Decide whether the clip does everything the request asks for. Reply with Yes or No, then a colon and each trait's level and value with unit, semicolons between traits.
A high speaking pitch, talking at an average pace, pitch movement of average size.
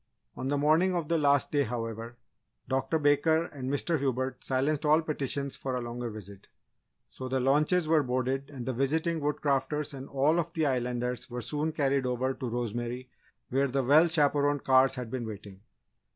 No: low, 135 Hz; average, 180 wpm; average, 3.1 semitones